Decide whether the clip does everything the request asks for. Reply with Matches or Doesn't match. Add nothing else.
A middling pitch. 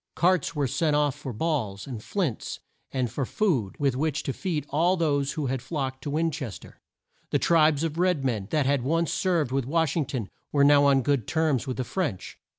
Matches